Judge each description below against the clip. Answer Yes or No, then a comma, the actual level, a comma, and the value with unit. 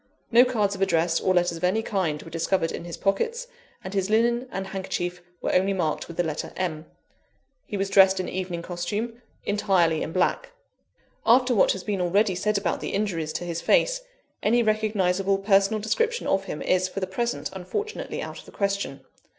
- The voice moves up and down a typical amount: Yes, average, 3.3 semitones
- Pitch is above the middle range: Yes, high, 195 Hz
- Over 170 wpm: Yes, average, 190 wpm